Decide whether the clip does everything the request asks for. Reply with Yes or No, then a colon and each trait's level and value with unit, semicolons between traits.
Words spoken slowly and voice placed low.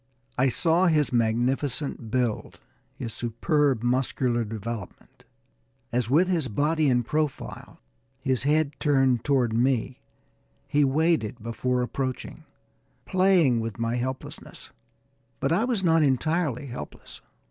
Yes: slow, 115 wpm; low, 130 Hz